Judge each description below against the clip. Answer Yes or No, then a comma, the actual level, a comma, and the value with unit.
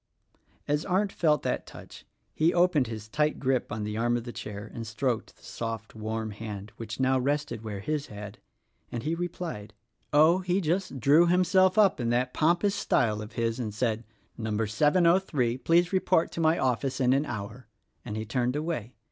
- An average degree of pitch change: No, wide, 6.8 semitones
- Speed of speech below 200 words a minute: No, fast, 205 wpm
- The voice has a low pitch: Yes, low, 130 Hz